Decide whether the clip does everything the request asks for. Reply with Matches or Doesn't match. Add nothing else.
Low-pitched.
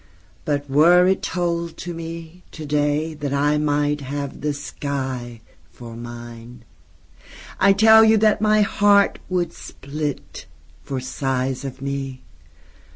Doesn't match